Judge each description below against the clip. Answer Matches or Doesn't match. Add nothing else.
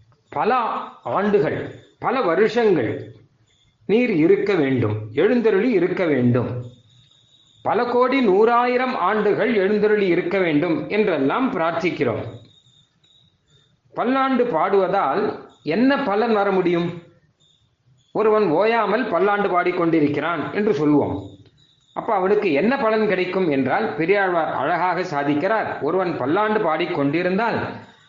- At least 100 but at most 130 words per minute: Doesn't match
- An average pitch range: Doesn't match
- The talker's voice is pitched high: Doesn't match